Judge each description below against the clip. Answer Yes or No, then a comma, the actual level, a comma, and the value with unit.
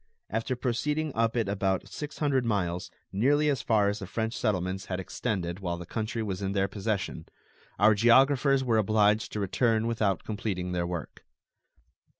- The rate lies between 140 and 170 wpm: Yes, average, 165 wpm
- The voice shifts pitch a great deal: No, average, 3.5 semitones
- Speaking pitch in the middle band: No, low, 105 Hz